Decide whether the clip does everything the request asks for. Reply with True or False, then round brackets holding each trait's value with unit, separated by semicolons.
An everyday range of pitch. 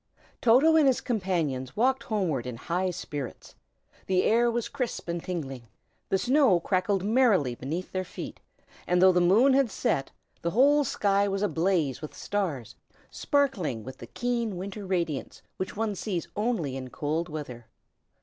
False (6.8 semitones)